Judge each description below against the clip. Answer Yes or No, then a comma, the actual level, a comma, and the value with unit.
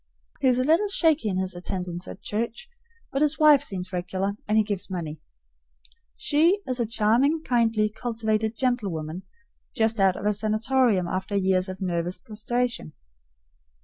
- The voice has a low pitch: No, high, 215 Hz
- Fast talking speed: No, average, 160 wpm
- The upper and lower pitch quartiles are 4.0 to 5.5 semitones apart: Yes, average, 5.1 semitones